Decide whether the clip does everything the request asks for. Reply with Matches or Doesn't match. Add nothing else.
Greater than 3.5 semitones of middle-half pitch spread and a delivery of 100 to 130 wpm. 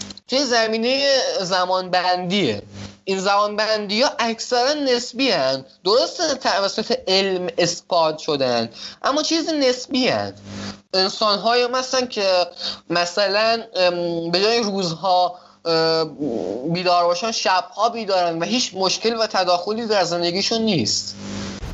Matches